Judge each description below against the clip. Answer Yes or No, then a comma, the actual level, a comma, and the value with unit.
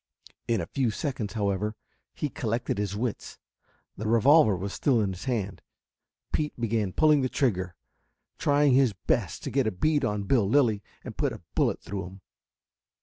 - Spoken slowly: No, average, 170 wpm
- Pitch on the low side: Yes, low, 115 Hz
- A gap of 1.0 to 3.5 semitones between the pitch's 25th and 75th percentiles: No, average, 5.1 semitones